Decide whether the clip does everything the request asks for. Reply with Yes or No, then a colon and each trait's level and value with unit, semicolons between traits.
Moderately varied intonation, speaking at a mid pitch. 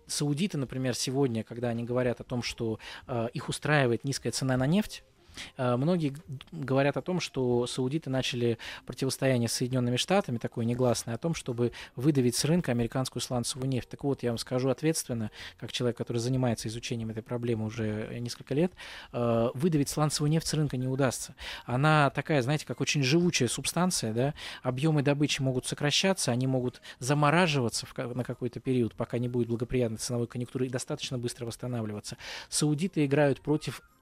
No: average, 3.3 semitones; low, 130 Hz